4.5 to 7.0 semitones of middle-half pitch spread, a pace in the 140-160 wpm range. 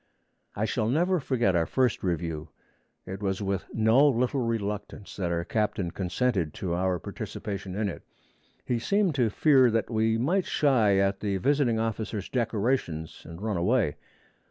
Yes: average, 4.8 semitones; average, 155 wpm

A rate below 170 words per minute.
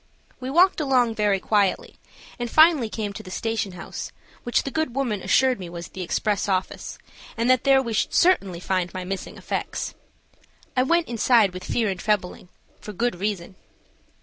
No: average, 175 wpm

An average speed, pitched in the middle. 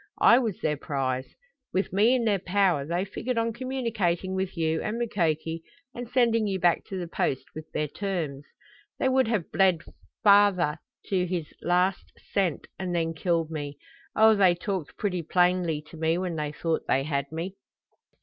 Yes: average, 175 wpm; medium, 180 Hz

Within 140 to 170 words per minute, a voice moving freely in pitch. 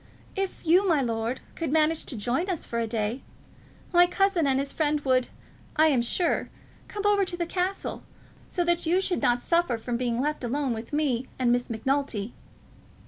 No: average, 190 wpm; wide, 6.2 semitones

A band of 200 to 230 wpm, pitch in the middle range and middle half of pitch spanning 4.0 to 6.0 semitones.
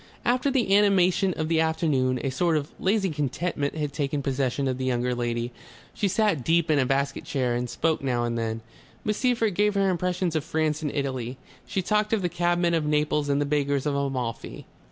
Yes: fast, 205 wpm; medium, 150 Hz; average, 5.1 semitones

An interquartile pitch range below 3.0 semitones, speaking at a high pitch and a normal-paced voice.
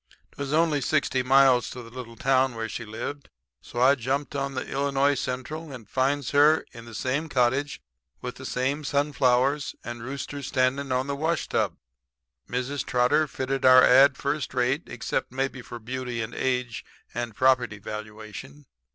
No: narrow, 2.4 semitones; low, 130 Hz; average, 165 wpm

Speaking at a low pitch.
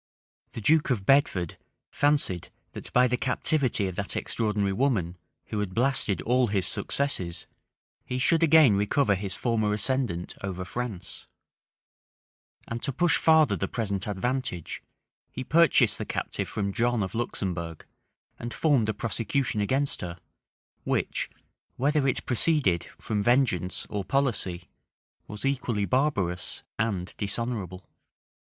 Yes: low, 115 Hz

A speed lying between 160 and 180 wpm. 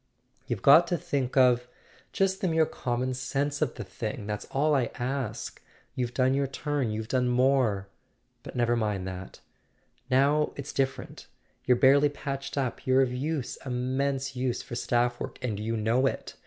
Yes: average, 170 wpm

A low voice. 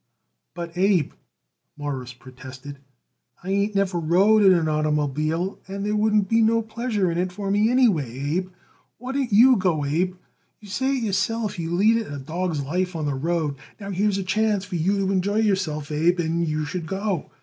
No: medium, 185 Hz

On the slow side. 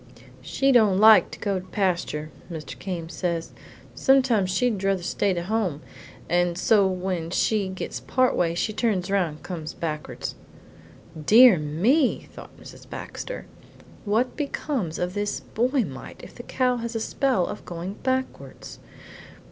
No: average, 150 wpm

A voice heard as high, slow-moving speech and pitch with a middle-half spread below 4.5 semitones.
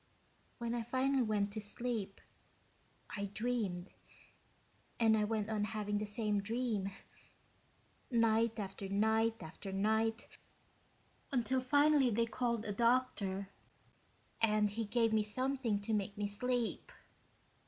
Yes: high, 220 Hz; slow, 120 wpm; narrow, 2.5 semitones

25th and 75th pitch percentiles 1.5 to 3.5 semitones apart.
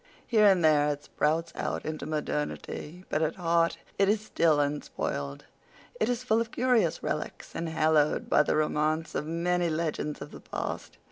Yes: average, 2.9 semitones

